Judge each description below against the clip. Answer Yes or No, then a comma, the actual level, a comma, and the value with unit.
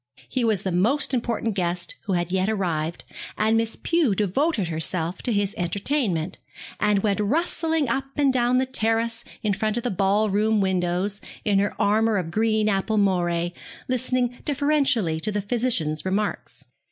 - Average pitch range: Yes, average, 4.2 semitones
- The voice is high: Yes, high, 210 Hz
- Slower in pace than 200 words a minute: Yes, average, 160 wpm